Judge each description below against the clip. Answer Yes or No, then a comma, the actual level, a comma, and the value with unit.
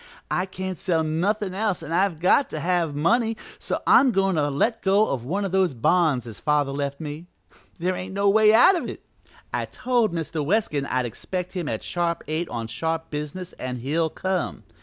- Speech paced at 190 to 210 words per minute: Yes, average, 200 wpm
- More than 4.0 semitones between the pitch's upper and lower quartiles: Yes, average, 4.6 semitones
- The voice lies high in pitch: No, medium, 175 Hz